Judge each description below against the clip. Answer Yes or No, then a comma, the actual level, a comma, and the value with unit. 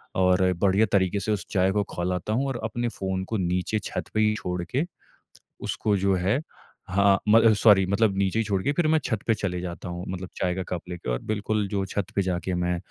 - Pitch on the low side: Yes, very low, 95 Hz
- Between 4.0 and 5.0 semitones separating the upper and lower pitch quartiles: No, average, 2.8 semitones